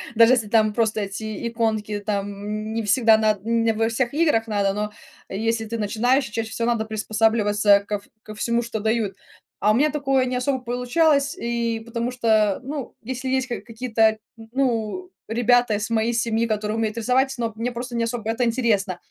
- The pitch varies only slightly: Yes, narrow, 2.2 semitones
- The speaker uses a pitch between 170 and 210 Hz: No, high, 225 Hz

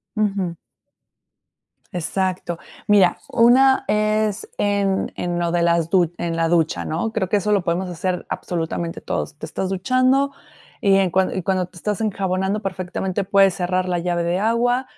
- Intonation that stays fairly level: No, average, 3.0 semitones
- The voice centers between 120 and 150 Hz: No, high, 190 Hz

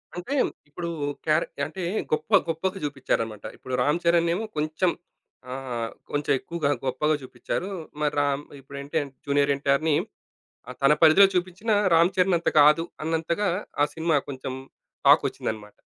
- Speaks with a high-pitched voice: No, medium, 155 Hz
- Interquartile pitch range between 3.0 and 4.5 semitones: Yes, average, 3.6 semitones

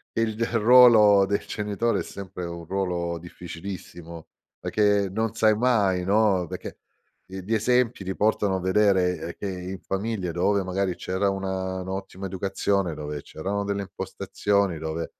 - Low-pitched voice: Yes, very low, 95 Hz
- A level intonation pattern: Yes, narrow, 2.3 semitones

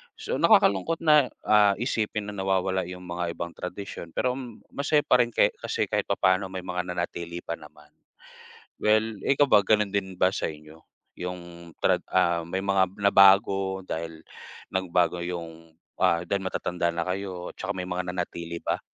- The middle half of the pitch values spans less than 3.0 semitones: Yes, narrow, 2.5 semitones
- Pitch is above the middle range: No, very low, 90 Hz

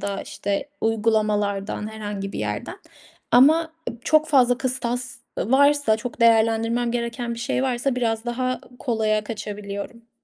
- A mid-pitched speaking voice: No, high, 230 Hz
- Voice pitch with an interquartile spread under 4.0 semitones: Yes, average, 2.8 semitones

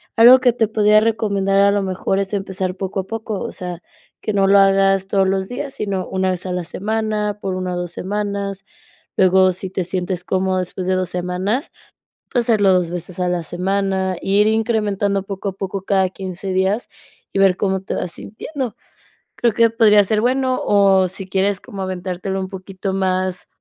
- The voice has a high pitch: Yes, high, 195 Hz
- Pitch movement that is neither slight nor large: No, narrow, 1.9 semitones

